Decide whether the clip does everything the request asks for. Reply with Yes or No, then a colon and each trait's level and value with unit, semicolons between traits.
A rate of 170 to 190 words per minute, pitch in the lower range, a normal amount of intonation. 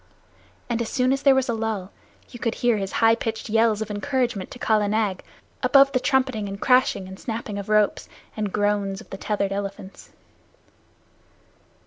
No: average, 175 wpm; high, 220 Hz; average, 3.3 semitones